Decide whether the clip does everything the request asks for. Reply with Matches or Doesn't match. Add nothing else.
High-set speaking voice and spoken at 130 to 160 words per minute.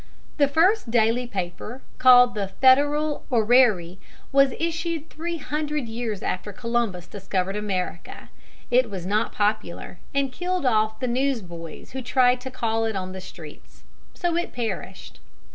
Matches